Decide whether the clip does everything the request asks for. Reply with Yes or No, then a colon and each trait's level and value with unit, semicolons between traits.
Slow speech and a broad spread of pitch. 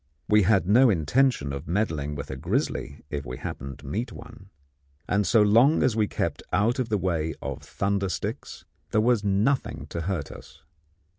No: average, 180 wpm; wide, 5.8 semitones